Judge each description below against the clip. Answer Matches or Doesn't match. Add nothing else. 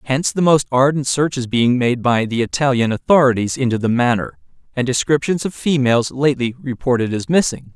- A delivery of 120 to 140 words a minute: Doesn't match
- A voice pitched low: Matches